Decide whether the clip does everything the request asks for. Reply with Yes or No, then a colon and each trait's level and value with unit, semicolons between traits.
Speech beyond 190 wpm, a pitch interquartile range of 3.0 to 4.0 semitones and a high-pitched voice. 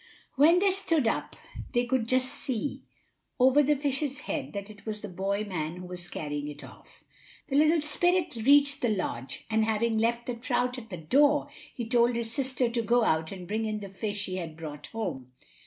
No: fast, 205 wpm; wide, 5.6 semitones; high, 230 Hz